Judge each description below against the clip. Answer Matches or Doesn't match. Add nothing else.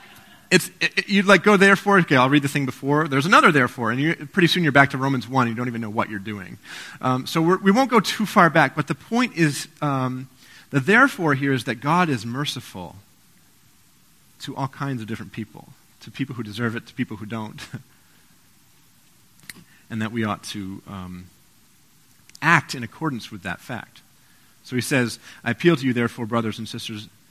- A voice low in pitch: Matches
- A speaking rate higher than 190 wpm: Matches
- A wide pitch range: Matches